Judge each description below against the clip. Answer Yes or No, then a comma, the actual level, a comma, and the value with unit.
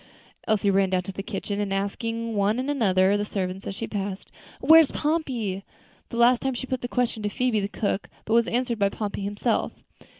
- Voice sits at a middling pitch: No, high, 210 Hz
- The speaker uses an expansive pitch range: No, average, 3.6 semitones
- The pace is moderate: No, fast, 210 wpm